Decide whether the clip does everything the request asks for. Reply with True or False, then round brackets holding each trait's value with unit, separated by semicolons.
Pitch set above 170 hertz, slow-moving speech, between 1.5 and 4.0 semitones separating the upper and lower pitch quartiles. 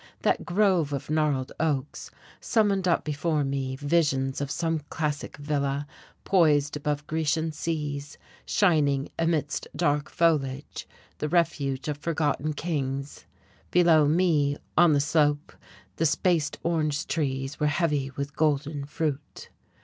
False (150 Hz; 125 wpm; 2.4 semitones)